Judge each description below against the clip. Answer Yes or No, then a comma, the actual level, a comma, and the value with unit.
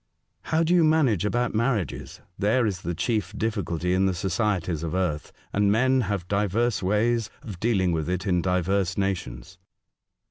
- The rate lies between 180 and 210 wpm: No, average, 170 wpm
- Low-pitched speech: Yes, low, 100 Hz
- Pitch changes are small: No, average, 3.9 semitones